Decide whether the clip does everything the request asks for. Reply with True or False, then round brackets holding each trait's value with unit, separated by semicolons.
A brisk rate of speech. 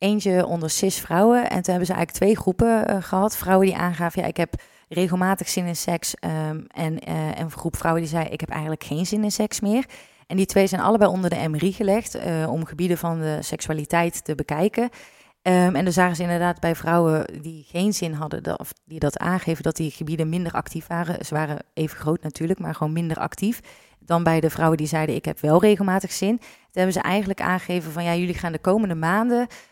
True (220 wpm)